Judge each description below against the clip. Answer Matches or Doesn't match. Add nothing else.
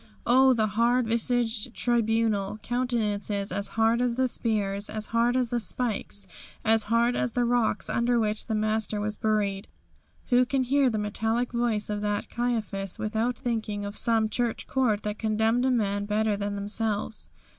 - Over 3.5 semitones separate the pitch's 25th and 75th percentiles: Doesn't match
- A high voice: Matches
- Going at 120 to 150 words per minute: Doesn't match